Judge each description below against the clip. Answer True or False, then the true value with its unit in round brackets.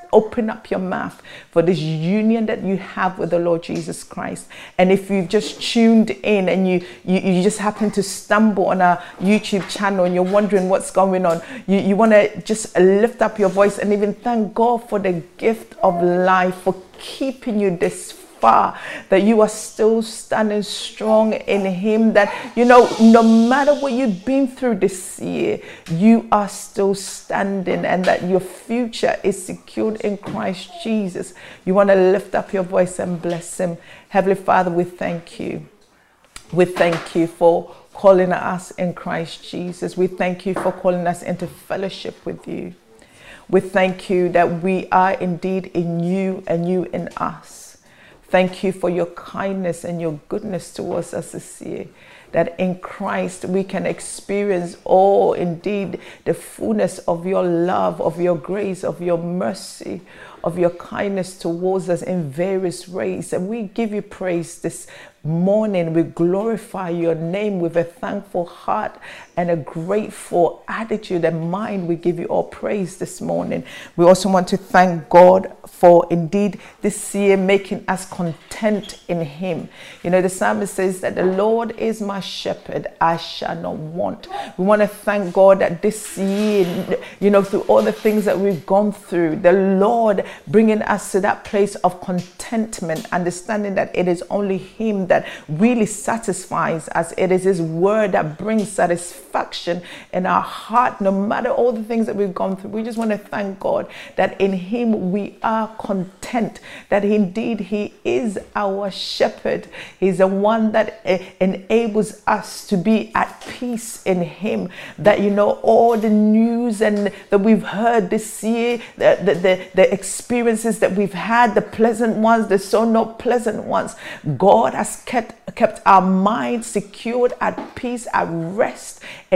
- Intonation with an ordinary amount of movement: True (3.0 semitones)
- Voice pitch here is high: True (195 Hz)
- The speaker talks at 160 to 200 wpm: True (170 wpm)